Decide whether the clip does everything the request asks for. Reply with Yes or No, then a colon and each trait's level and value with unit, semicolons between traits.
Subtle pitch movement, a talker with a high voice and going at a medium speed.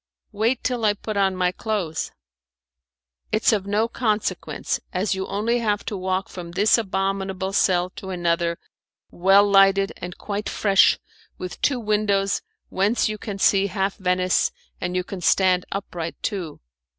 Yes: narrow, 2.3 semitones; high, 195 Hz; average, 150 wpm